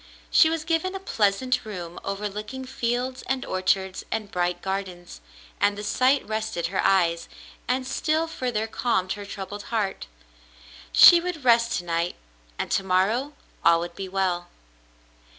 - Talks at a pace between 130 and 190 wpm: Yes, average, 150 wpm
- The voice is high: Yes, high, 205 Hz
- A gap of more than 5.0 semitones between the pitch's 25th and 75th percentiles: Yes, wide, 5.4 semitones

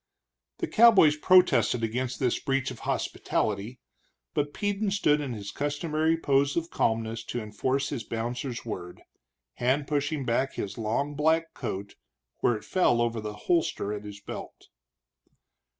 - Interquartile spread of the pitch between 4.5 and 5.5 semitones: Yes, average, 5.0 semitones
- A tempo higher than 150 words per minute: No, average, 145 wpm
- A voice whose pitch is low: Yes, low, 130 Hz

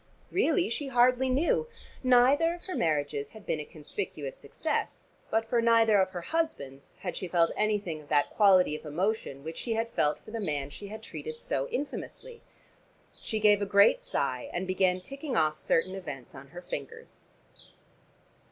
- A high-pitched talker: Yes, high, 195 Hz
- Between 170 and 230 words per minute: Yes, average, 175 wpm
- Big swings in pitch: Yes, wide, 7.8 semitones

